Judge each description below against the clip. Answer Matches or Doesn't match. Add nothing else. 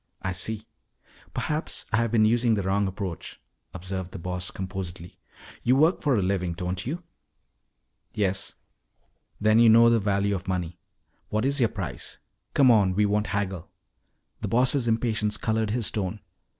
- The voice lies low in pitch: Matches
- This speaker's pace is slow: Doesn't match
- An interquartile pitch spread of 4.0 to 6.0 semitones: Doesn't match